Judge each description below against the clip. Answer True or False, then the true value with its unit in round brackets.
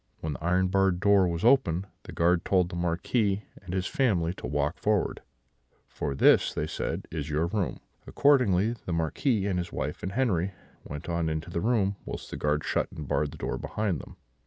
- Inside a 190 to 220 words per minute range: True (200 wpm)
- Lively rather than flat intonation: False (3.4 semitones)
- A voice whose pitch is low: True (90 Hz)